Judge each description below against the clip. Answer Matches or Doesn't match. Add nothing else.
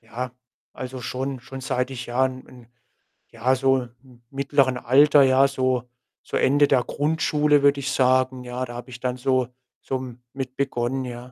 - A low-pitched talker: Matches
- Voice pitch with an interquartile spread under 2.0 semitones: Matches